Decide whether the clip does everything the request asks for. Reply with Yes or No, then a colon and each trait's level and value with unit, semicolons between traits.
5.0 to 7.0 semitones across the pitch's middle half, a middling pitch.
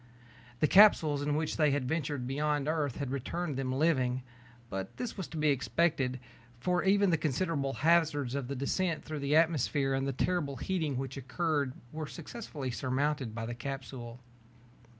No: average, 3.5 semitones; medium, 145 Hz